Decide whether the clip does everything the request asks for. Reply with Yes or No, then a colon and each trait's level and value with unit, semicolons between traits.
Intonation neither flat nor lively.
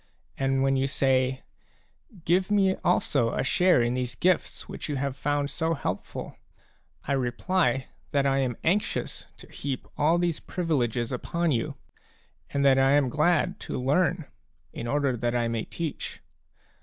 Yes: average, 4.6 semitones